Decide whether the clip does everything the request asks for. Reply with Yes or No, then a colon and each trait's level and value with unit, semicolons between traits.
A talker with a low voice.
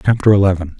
Yes: very low, 95 Hz